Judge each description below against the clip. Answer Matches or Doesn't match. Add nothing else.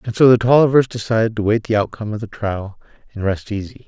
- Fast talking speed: Matches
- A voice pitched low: Matches